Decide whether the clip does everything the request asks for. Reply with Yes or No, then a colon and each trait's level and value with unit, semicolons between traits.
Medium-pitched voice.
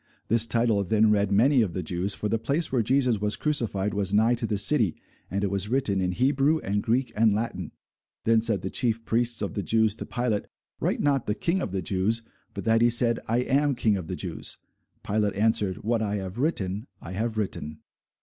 No: low, 110 Hz